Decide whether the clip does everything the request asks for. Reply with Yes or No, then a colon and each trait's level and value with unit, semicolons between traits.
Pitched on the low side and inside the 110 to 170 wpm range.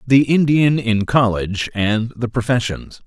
Yes: low, 120 Hz; slow, 135 wpm